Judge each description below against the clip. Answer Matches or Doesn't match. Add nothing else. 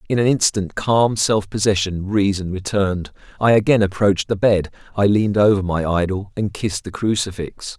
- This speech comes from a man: Matches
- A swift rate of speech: Doesn't match